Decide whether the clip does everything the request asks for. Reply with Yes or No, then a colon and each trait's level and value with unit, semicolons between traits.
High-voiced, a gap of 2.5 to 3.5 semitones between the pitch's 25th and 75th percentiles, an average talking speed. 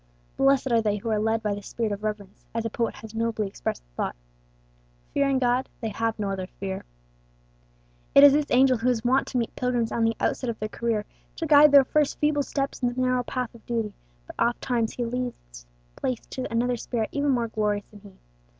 No: high, 230 Hz; average, 3.0 semitones; fast, 215 wpm